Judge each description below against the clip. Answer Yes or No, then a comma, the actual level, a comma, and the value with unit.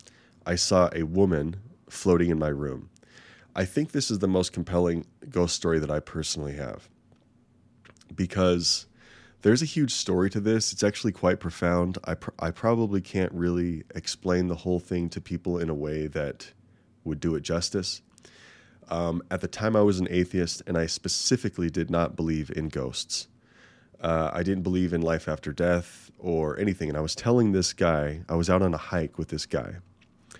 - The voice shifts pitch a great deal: No, average, 3.1 semitones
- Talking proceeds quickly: No, average, 185 wpm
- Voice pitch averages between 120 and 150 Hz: No, very low, 90 Hz